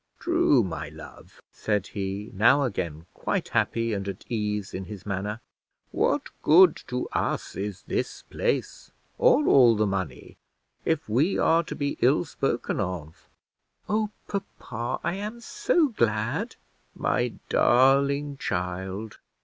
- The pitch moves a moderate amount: No, wide, 7.6 semitones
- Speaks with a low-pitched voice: Yes, low, 115 Hz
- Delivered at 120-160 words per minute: Yes, slow, 135 wpm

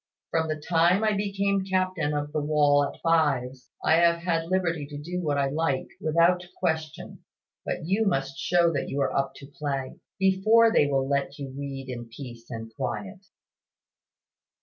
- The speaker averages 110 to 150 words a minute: No, average, 170 wpm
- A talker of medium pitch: Yes, medium, 155 Hz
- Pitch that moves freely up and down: No, average, 4.3 semitones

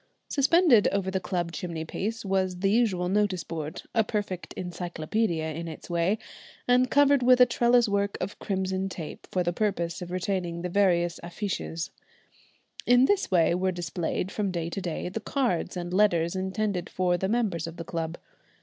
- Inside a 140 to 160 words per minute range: No, average, 175 wpm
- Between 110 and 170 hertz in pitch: No, medium, 185 Hz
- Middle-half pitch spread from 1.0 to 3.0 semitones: No, average, 3.5 semitones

